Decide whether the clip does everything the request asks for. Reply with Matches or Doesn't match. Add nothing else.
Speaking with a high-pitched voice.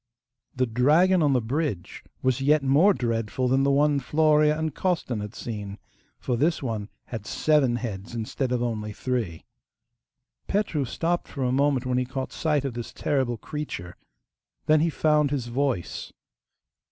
Doesn't match